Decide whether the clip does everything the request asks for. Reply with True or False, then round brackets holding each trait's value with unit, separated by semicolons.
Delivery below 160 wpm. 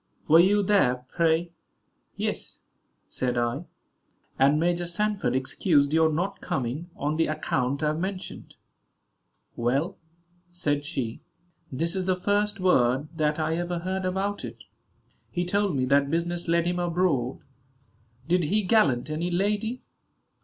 True (140 wpm)